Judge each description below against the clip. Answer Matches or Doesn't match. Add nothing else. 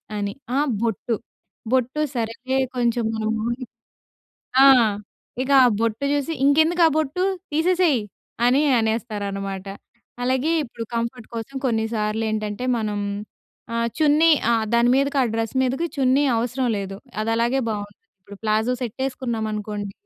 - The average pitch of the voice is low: Doesn't match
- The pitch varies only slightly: Doesn't match